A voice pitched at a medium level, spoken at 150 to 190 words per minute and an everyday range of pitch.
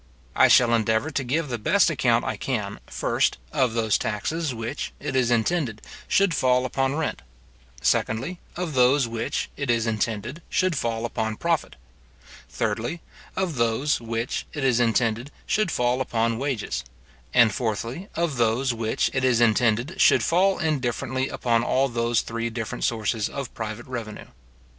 No: low, 120 Hz; average, 155 wpm; average, 3.5 semitones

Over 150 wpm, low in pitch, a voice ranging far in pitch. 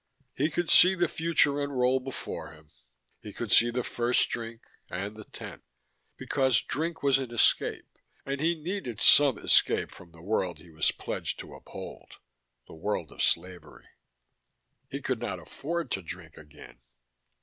Yes: average, 160 wpm; low, 120 Hz; wide, 7.5 semitones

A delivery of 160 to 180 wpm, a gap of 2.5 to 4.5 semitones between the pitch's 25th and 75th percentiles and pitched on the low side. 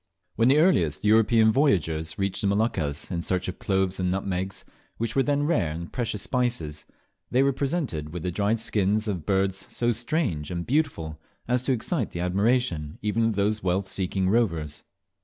No: average, 175 wpm; average, 5.3 semitones; low, 100 Hz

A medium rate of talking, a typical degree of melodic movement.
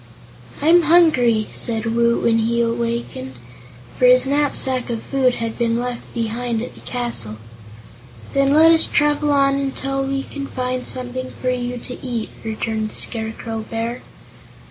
Yes: average, 150 wpm; average, 3.0 semitones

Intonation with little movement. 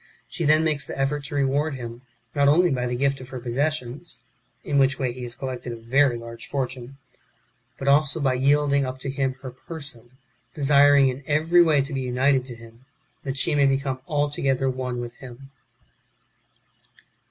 Yes: narrow, 2.3 semitones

